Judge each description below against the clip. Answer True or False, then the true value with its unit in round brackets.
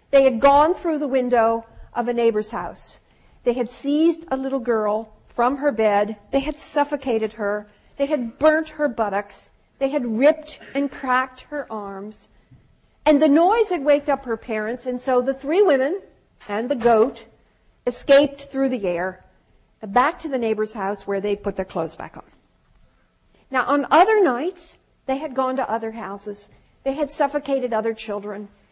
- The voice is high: True (255 Hz)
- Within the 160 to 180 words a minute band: True (170 wpm)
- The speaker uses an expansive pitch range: False (4.8 semitones)